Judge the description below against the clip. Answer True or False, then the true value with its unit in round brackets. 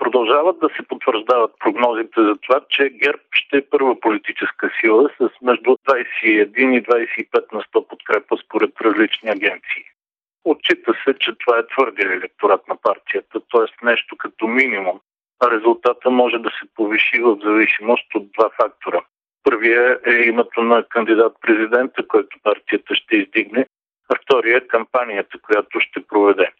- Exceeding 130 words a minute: True (145 wpm)